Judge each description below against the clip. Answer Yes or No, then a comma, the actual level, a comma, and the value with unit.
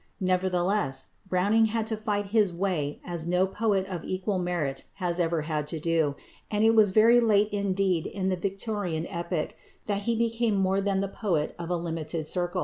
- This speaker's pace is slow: No, average, 185 wpm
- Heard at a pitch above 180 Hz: Yes, high, 190 Hz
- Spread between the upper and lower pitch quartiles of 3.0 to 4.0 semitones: Yes, average, 3.3 semitones